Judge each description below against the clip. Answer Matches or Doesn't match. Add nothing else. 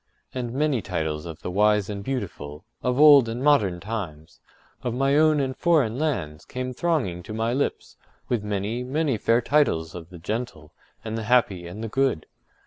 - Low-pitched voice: Matches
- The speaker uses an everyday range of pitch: Doesn't match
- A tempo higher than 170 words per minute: Matches